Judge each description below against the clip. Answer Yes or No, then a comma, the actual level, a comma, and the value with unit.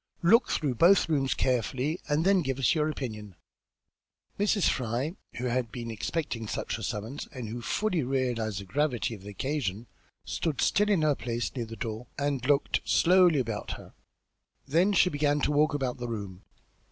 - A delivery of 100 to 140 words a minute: No, average, 180 wpm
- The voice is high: No, low, 130 Hz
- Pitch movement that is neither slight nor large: Yes, average, 5.0 semitones